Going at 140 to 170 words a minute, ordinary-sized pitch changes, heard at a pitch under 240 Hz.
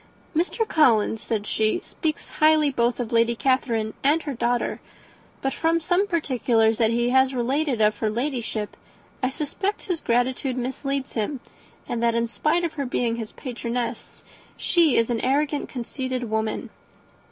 No: average, 155 wpm; average, 4.1 semitones; very high, 250 Hz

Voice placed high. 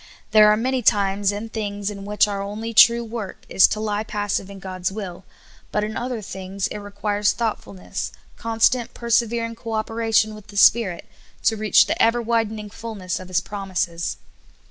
Yes: high, 210 Hz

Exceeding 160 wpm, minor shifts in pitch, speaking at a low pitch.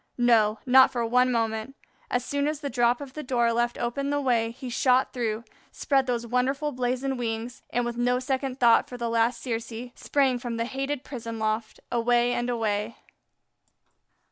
No: average, 185 wpm; narrow, 2.1 semitones; high, 245 Hz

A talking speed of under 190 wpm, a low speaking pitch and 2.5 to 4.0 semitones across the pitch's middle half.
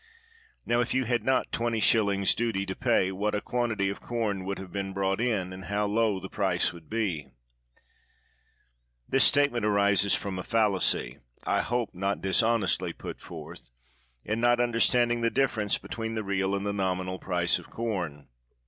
Yes: average, 175 wpm; low, 100 Hz; average, 3.5 semitones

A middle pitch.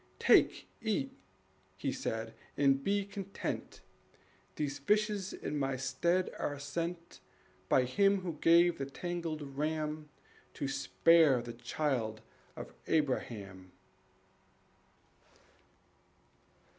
Yes: medium, 150 Hz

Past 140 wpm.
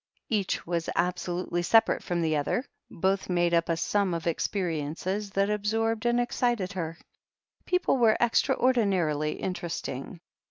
No: slow, 135 wpm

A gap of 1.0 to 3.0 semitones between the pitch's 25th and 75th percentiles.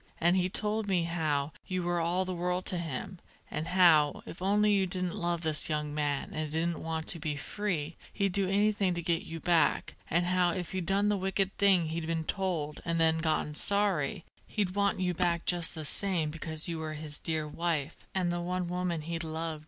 Yes: narrow, 2.6 semitones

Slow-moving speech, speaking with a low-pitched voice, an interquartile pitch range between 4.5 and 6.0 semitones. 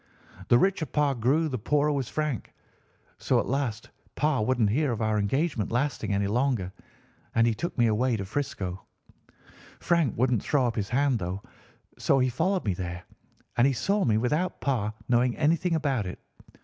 No: average, 175 wpm; low, 125 Hz; average, 5.2 semitones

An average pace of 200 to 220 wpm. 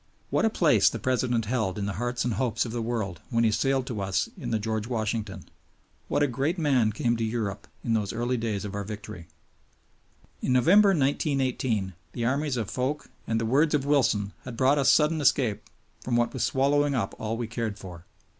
Yes: fast, 205 wpm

